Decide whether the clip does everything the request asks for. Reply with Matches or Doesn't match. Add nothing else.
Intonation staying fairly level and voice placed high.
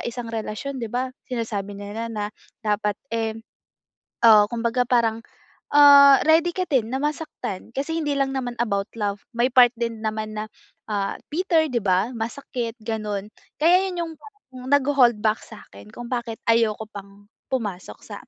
Doesn't match